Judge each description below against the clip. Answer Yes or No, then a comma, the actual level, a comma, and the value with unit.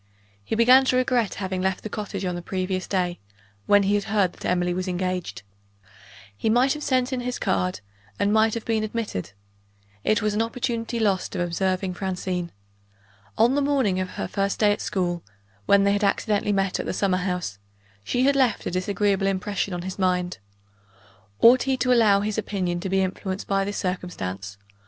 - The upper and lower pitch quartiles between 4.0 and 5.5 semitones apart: No, average, 3.3 semitones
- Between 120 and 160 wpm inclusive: No, average, 190 wpm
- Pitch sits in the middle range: No, high, 195 Hz